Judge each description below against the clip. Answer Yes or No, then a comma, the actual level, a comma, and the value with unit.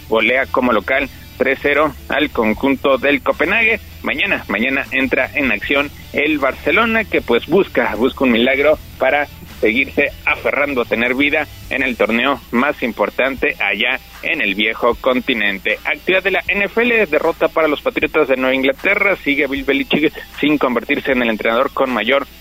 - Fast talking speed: No, average, 155 wpm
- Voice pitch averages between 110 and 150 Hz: Yes, medium, 140 Hz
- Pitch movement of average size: Yes, average, 3.7 semitones